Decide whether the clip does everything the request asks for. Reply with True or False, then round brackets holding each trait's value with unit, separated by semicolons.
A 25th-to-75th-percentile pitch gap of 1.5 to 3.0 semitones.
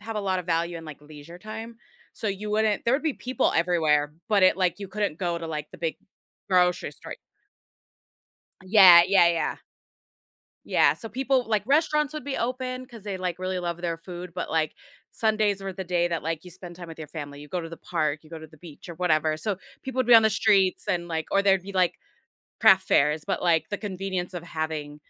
False (4.2 semitones)